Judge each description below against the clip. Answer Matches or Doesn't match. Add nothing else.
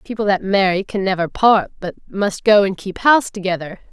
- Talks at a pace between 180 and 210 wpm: Matches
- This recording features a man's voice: Doesn't match